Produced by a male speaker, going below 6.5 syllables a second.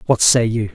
Yes: male; 5.2 syllables/s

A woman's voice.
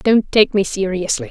Yes: female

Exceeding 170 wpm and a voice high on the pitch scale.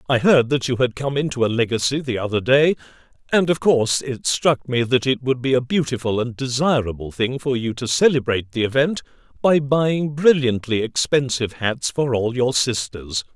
No: average, 190 wpm; low, 130 Hz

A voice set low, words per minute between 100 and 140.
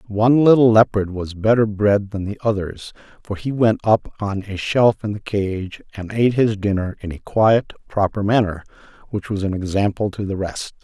No: low, 105 Hz; average, 195 wpm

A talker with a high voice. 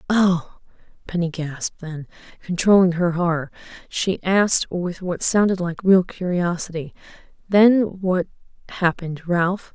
No: medium, 180 Hz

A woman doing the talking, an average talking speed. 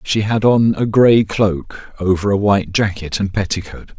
No: male; average, 180 wpm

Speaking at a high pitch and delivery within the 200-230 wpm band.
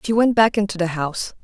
No: high, 195 Hz; fast, 250 wpm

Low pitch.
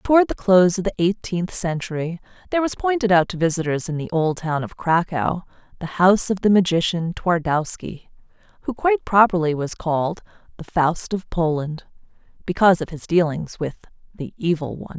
No: medium, 180 Hz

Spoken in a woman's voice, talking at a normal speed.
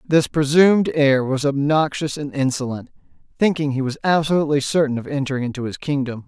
No: male; average, 165 wpm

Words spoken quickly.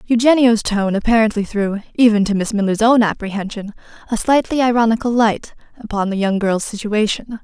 No: average, 155 wpm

